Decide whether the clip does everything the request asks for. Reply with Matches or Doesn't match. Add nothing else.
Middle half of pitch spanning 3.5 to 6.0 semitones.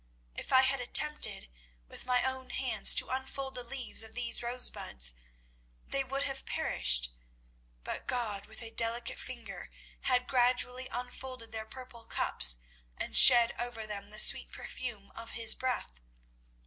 Doesn't match